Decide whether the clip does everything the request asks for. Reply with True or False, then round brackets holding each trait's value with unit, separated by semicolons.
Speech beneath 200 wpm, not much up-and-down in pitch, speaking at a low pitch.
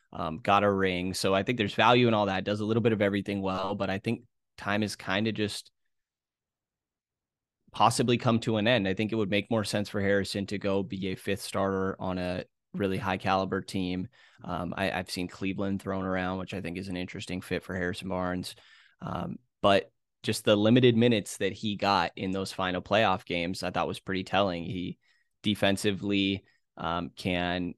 False (205 wpm; 1.9 semitones; 95 Hz)